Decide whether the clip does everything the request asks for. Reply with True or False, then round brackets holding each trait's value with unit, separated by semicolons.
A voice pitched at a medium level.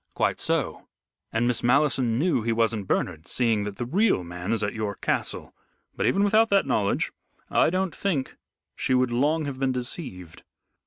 False (125 Hz)